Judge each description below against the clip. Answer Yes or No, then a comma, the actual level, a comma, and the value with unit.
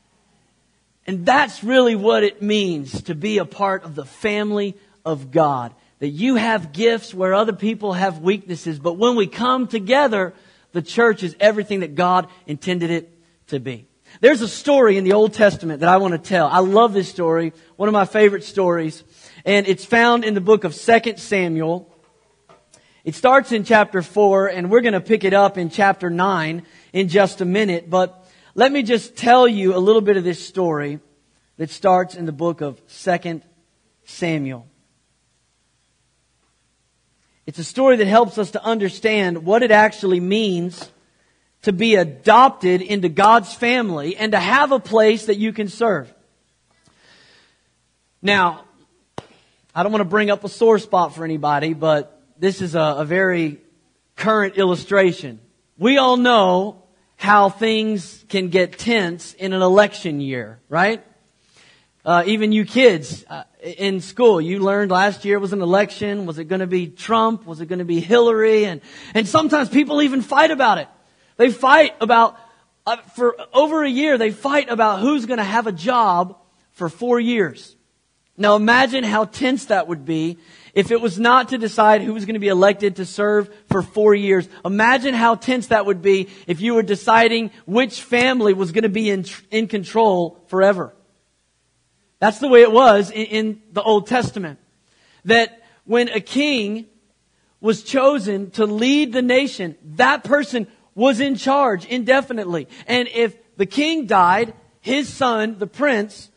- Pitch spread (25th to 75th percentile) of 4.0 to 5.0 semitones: Yes, average, 4.3 semitones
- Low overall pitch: No, high, 205 Hz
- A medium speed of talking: Yes, average, 170 wpm